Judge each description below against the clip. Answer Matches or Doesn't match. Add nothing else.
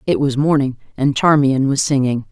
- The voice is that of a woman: Matches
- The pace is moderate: Matches